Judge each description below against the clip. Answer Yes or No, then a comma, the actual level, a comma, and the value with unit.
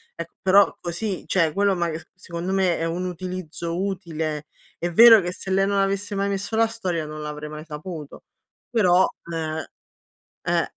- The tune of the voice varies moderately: Yes, average, 3.3 semitones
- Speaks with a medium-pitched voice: Yes, medium, 180 Hz